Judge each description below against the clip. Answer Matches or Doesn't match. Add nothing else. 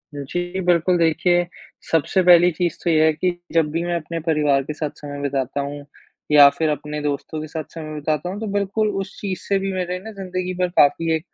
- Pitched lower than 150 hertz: Doesn't match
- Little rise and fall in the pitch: Doesn't match